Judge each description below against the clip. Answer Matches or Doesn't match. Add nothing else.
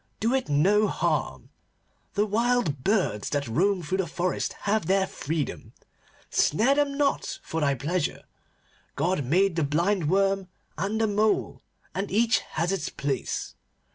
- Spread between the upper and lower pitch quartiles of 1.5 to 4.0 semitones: Doesn't match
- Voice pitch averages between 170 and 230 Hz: Matches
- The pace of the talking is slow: Doesn't match